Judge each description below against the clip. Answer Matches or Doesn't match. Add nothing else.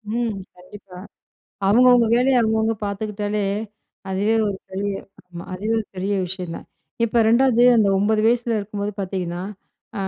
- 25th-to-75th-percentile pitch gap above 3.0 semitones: Doesn't match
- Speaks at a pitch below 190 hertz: Doesn't match